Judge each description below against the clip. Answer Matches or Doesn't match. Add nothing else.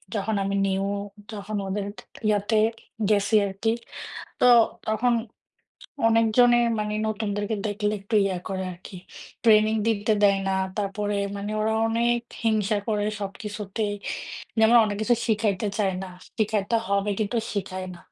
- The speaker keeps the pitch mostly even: Matches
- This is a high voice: Matches